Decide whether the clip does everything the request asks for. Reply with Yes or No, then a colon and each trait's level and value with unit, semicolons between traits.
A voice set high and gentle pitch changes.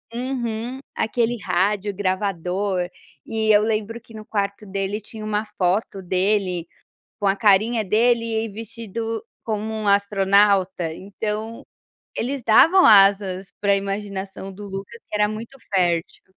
Yes: high, 205 Hz; narrow, 2.3 semitones